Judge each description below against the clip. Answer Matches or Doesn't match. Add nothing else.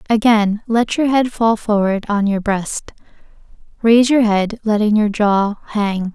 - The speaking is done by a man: Doesn't match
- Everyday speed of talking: Matches